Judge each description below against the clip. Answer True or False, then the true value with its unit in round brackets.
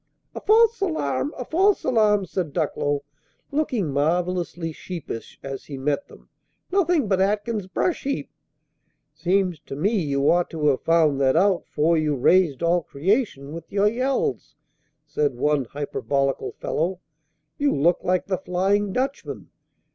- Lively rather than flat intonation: True (6.2 semitones)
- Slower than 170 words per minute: True (145 wpm)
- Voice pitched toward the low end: False (180 Hz)